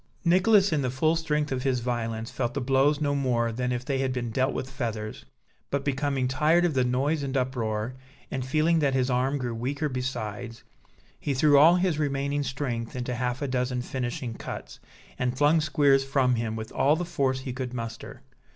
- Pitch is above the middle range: No, low, 130 Hz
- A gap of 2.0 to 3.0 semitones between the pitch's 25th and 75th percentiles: Yes, narrow, 2.6 semitones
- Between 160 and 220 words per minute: Yes, average, 195 wpm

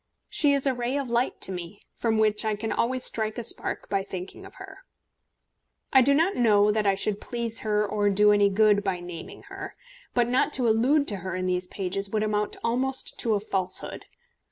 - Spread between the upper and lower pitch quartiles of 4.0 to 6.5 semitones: No, average, 3.6 semitones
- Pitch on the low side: No, high, 215 Hz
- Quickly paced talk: Yes, fast, 210 wpm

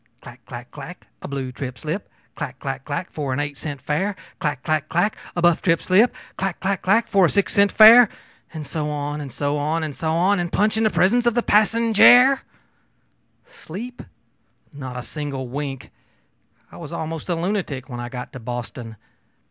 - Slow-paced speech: No, average, 190 wpm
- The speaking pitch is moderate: Yes, medium, 160 Hz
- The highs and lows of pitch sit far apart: Yes, wide, 6.3 semitones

